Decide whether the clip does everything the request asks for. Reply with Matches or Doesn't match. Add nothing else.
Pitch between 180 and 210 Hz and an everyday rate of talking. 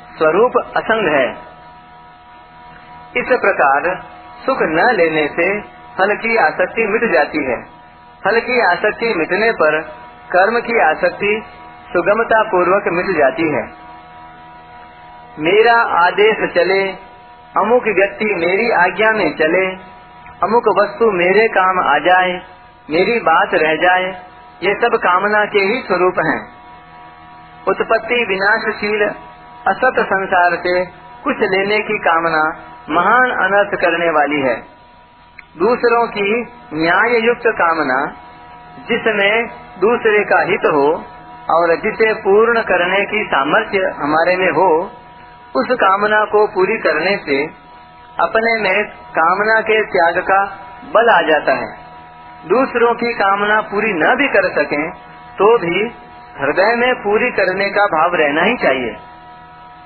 Matches